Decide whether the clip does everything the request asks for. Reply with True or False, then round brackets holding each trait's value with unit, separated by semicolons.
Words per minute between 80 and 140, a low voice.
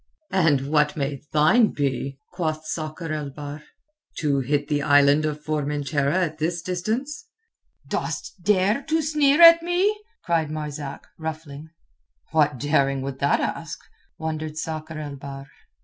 False (135 wpm; 155 Hz)